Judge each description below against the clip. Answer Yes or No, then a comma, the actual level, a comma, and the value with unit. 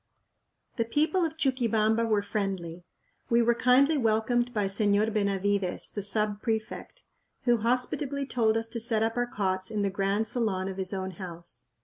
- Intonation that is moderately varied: Yes, average, 3.3 semitones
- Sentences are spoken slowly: No, average, 165 wpm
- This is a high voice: Yes, high, 220 Hz